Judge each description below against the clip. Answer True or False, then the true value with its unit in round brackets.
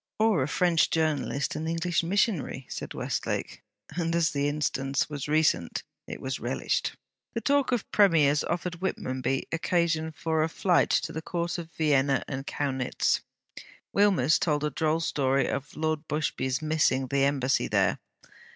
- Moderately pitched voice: True (155 Hz)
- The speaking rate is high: False (150 wpm)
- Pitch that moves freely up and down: False (3.4 semitones)